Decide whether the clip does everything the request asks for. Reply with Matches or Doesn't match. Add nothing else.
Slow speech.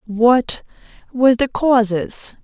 Matches